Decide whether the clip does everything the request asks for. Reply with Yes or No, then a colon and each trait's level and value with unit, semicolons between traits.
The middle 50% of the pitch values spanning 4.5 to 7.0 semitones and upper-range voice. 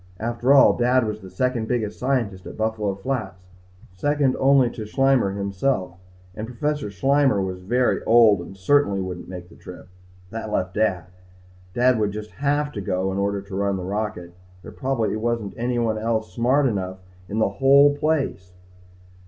No: average, 4.8 semitones; low, 110 Hz